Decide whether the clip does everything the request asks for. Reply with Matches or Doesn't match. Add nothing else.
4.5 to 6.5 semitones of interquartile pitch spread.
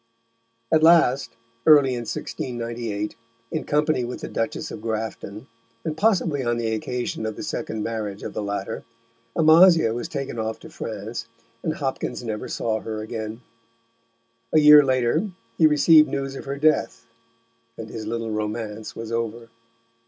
Matches